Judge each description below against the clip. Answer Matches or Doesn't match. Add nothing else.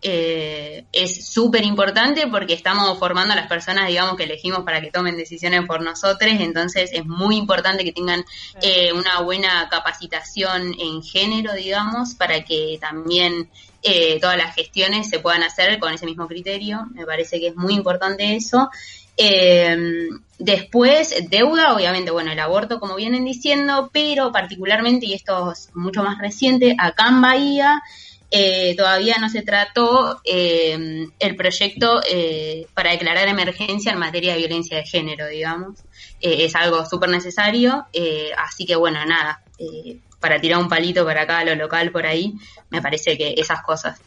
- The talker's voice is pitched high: Doesn't match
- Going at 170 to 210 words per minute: Doesn't match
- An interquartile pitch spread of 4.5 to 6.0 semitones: Doesn't match